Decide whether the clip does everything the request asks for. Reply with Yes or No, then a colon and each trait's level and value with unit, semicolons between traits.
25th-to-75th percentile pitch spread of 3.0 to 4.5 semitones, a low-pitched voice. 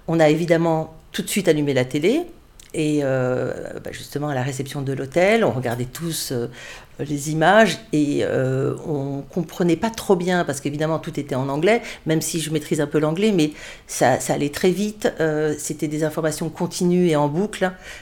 No: average, 3.7 semitones; medium, 155 Hz